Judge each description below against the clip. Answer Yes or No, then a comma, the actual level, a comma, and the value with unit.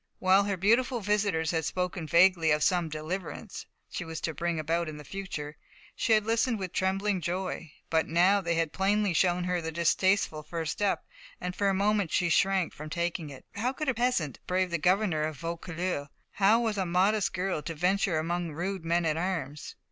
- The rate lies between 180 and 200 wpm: Yes, average, 195 wpm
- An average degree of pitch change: Yes, average, 3.3 semitones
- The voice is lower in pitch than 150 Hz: No, medium, 180 Hz